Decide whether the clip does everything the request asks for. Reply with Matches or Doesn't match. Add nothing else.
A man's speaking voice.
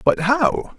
Matches